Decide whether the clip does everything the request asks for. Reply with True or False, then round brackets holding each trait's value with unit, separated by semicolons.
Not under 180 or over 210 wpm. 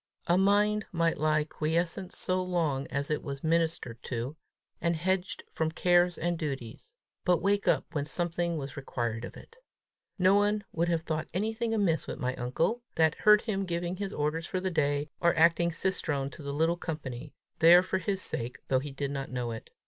True (190 wpm)